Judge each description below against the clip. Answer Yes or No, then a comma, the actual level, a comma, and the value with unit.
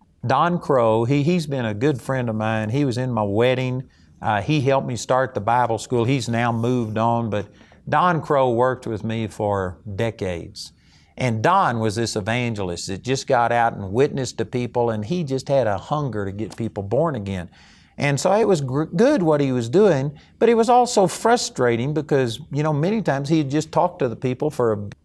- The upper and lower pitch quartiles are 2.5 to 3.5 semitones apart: No, average, 5.1 semitones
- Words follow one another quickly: Yes, fast, 210 wpm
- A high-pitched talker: No, low, 125 Hz